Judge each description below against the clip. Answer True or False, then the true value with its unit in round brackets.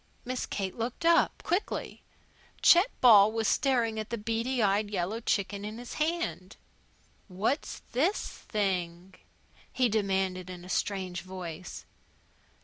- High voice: True (210 Hz)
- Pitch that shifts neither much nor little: True (4.4 semitones)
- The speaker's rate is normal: False (130 wpm)